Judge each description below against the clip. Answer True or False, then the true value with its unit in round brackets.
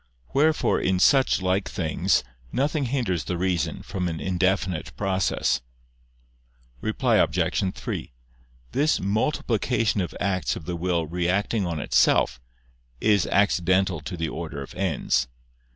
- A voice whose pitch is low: True (95 Hz)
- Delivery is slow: True (125 wpm)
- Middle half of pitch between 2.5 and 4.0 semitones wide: True (3.0 semitones)